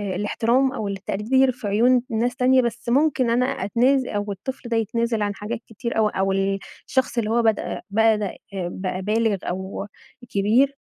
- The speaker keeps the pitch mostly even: No, average, 3.4 semitones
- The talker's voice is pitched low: No, high, 225 Hz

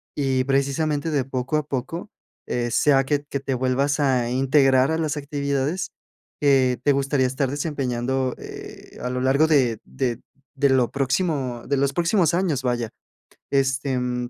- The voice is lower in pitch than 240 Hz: Yes, low, 135 Hz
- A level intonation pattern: Yes, narrow, 2.1 semitones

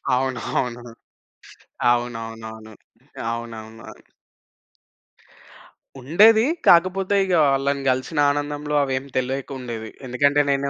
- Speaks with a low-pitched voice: Yes, low, 130 Hz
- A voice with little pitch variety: No, average, 3.7 semitones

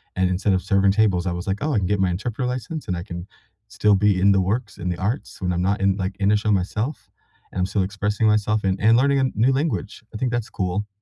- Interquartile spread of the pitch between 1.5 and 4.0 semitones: Yes, average, 2.7 semitones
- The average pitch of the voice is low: Yes, low, 100 Hz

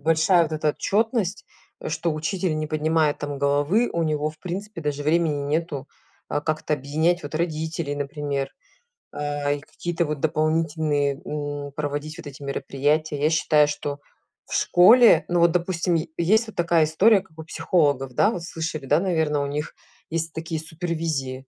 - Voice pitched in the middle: Yes, medium, 155 Hz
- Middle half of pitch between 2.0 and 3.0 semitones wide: Yes, narrow, 2.5 semitones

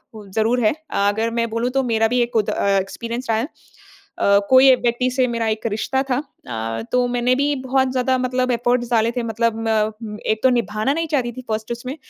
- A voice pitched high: Yes, high, 235 Hz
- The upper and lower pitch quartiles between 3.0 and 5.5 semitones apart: No, narrow, 2.4 semitones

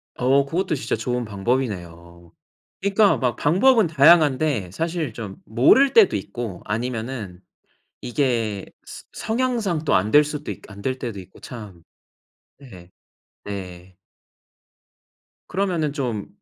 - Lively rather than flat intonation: Yes, wide, 7.5 semitones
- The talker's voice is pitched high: No, low, 125 Hz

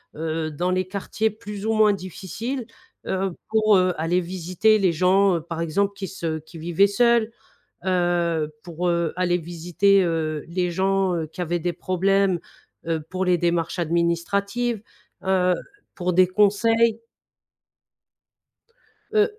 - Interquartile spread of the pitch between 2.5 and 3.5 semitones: Yes, average, 2.8 semitones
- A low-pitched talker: No, medium, 185 Hz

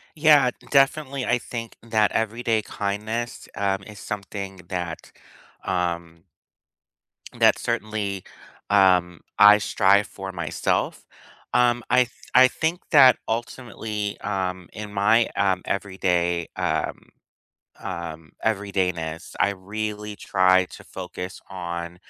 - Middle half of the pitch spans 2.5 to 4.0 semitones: Yes, average, 3.5 semitones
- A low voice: Yes, low, 100 Hz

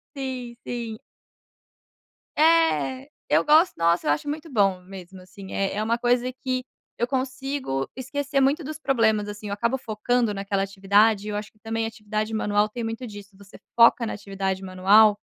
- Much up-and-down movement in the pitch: No, average, 4.3 semitones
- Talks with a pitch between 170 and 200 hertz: No, high, 220 Hz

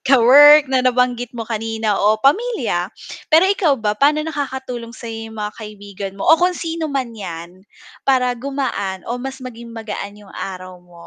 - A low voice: No, high, 240 Hz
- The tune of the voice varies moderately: Yes, average, 4.8 semitones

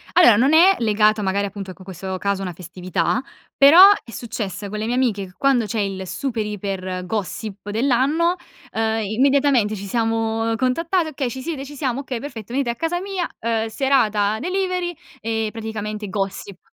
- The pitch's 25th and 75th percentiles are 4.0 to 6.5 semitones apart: Yes, average, 5.0 semitones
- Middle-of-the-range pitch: No, high, 225 Hz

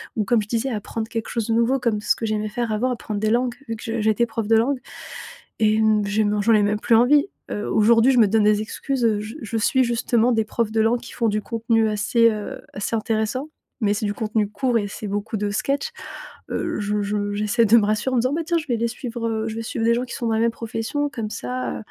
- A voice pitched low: No, high, 225 Hz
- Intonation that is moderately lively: No, narrow, 1.9 semitones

